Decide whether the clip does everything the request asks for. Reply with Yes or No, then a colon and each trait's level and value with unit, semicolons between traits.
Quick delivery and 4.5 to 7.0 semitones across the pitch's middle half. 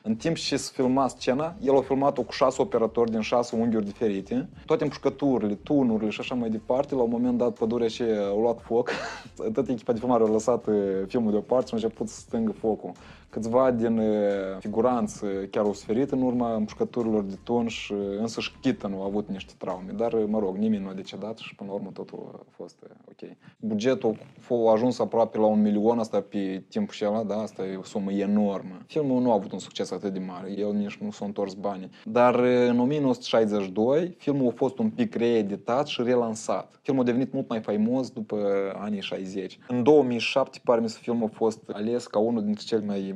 No: fast, 210 wpm; average, 4.0 semitones